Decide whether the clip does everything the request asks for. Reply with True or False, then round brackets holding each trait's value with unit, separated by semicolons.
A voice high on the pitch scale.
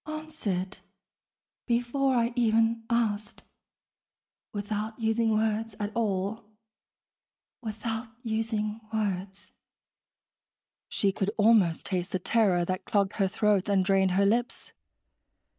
True (215 Hz)